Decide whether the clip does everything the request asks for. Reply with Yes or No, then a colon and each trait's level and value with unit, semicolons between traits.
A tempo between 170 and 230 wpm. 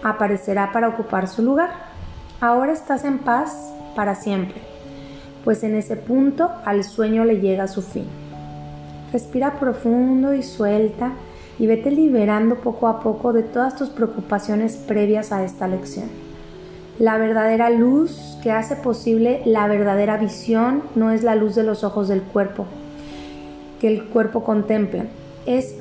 No: average, 145 wpm